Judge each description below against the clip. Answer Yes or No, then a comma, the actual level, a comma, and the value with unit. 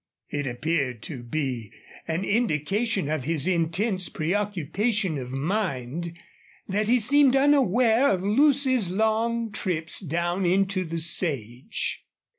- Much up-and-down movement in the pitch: Yes, wide, 5.9 semitones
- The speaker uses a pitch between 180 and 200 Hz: Yes, medium, 185 Hz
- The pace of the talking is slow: Yes, slow, 115 wpm